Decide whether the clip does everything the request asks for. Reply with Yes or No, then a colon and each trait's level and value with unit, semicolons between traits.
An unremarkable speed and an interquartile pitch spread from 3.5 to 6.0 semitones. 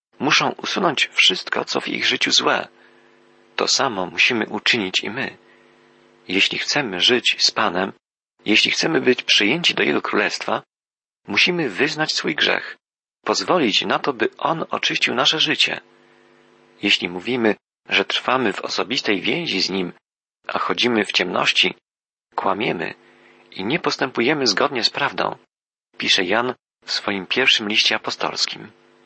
Yes: average, 135 wpm; average, 4.2 semitones